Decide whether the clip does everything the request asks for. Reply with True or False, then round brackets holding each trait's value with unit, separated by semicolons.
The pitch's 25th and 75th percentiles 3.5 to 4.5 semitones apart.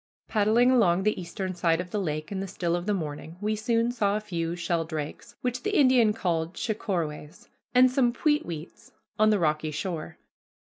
False (5.1 semitones)